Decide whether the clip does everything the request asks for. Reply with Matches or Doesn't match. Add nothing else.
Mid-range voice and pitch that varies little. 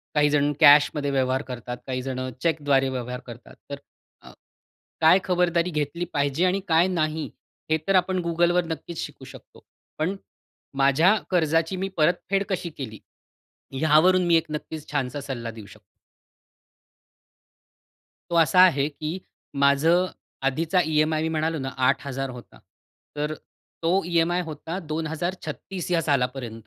Doesn't match